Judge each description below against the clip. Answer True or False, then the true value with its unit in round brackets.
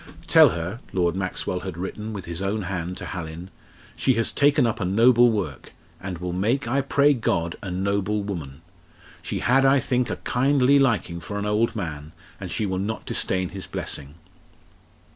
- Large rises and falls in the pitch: False (4.8 semitones)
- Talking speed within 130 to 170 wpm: False (180 wpm)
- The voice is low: True (100 Hz)